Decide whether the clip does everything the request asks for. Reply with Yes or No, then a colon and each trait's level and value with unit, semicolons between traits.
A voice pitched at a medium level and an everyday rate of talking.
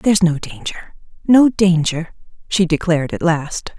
No: medium, 170 Hz; slow, 125 wpm